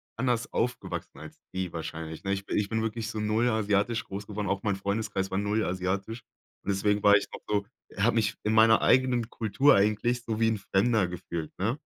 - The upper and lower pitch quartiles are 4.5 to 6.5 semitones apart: No, narrow, 2.4 semitones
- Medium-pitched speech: No, low, 105 Hz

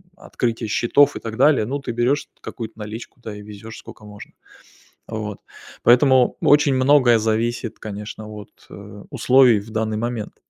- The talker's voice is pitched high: No, low, 115 Hz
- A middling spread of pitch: Yes, average, 3.0 semitones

